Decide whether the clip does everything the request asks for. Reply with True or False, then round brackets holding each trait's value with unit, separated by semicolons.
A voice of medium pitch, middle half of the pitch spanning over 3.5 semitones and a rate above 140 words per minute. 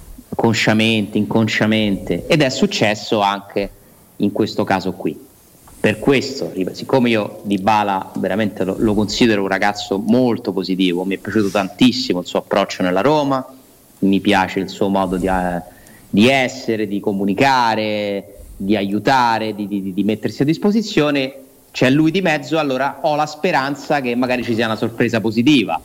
False (110 Hz; 4.3 semitones; 155 wpm)